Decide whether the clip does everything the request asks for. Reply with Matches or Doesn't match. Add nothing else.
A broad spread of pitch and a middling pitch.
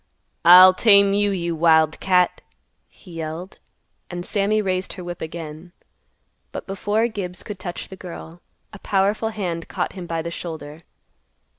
Doesn't match